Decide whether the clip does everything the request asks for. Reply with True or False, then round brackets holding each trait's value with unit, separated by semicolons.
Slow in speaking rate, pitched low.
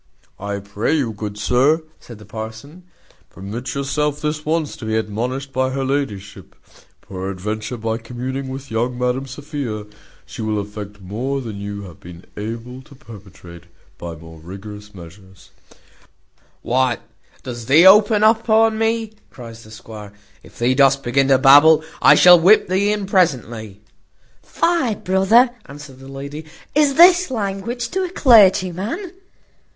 False (145 wpm; 130 Hz)